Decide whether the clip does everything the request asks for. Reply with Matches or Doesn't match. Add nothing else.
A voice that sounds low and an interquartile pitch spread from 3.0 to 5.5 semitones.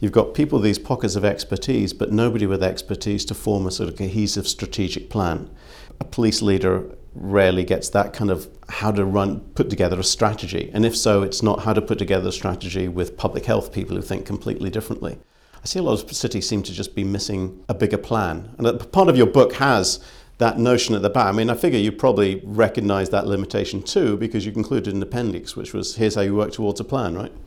Doesn't match